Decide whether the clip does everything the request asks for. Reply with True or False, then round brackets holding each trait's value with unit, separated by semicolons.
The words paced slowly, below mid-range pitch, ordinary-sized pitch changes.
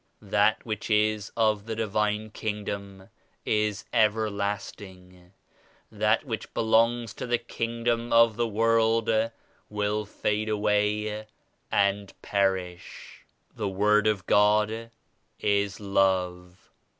False (110 wpm; 105 Hz; 1.7 semitones)